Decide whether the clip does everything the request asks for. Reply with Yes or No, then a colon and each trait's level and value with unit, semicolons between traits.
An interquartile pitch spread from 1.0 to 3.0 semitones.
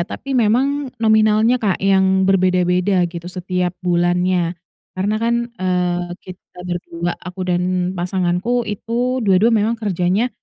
No: average, 3.4 semitones